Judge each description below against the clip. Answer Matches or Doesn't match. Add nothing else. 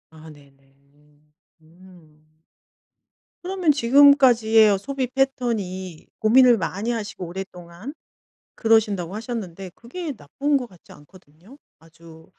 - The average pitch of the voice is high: Matches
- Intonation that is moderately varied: Doesn't match